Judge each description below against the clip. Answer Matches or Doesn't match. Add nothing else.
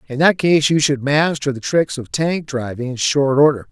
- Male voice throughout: Matches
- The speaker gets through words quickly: Matches